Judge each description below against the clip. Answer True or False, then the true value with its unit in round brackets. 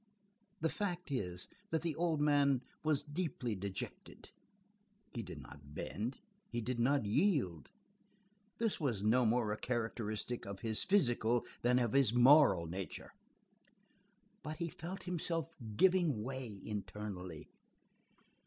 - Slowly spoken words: True (125 wpm)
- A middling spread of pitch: False (6.5 semitones)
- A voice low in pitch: True (125 Hz)